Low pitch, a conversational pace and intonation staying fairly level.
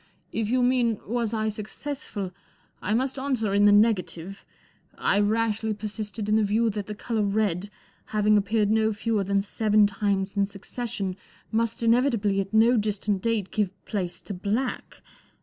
No: high, 210 Hz; average, 165 wpm; narrow, 2.1 semitones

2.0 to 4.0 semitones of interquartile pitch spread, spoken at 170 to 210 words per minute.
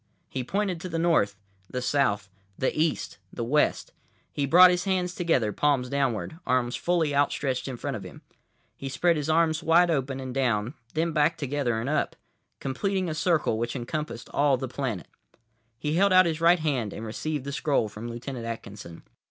No: average, 5.0 semitones; average, 185 wpm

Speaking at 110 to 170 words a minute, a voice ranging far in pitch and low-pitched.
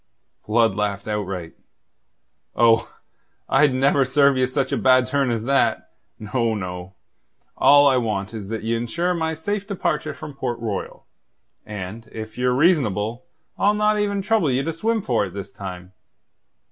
Yes: average, 160 wpm; wide, 5.7 semitones; low, 125 Hz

